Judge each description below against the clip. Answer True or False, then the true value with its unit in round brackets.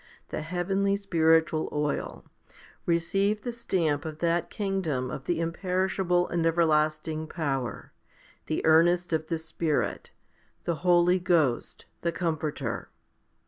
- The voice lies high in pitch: False (165 Hz)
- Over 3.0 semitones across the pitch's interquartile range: False (2.4 semitones)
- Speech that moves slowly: True (115 wpm)